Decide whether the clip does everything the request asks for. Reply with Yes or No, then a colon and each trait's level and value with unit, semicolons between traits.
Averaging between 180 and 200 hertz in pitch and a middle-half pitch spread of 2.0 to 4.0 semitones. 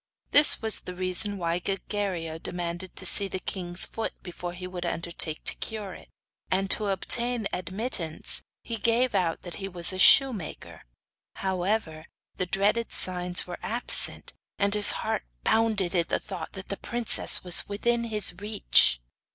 Yes: high, 190 Hz; average, 3.2 semitones